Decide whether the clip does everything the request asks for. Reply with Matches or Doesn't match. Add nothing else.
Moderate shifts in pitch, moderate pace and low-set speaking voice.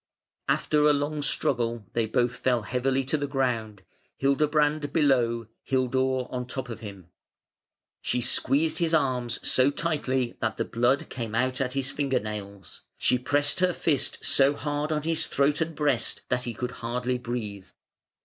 Matches